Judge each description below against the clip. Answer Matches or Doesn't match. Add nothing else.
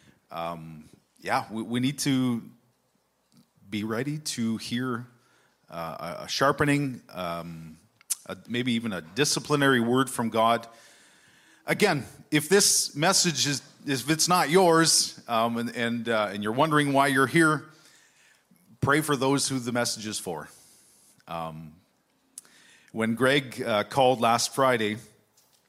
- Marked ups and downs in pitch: Doesn't match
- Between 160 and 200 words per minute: Doesn't match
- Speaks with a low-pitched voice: Matches